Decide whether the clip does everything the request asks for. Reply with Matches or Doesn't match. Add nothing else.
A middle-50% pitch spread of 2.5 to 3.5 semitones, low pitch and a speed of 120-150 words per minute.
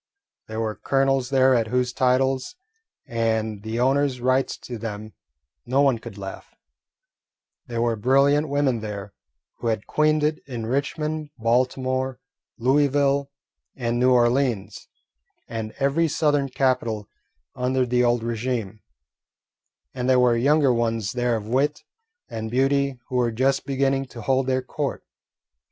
Matches